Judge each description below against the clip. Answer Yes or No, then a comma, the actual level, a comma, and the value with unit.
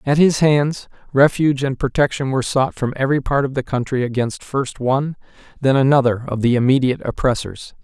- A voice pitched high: No, low, 135 Hz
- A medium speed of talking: Yes, average, 175 wpm